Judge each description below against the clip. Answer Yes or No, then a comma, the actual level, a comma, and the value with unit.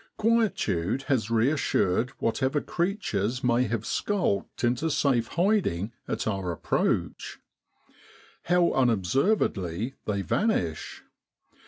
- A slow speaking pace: Yes, slow, 95 wpm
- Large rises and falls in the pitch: Yes, wide, 8.6 semitones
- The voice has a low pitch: Yes, low, 120 Hz